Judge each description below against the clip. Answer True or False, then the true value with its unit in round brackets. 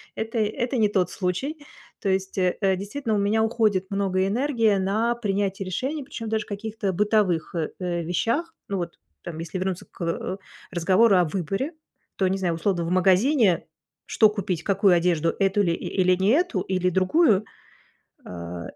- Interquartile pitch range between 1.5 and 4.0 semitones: True (3.4 semitones)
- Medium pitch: False (195 Hz)